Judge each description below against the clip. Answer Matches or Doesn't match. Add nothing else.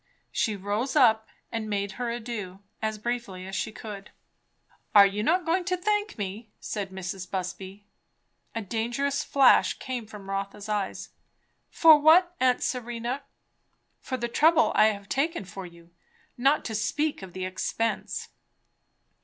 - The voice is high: Matches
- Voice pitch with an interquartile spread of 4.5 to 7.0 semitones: Matches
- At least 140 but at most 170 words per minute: Matches